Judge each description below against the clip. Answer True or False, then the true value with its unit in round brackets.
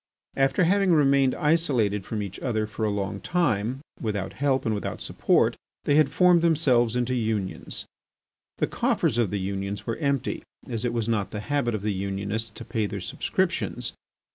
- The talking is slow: False (175 wpm)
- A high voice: False (115 Hz)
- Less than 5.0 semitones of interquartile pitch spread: False (5.3 semitones)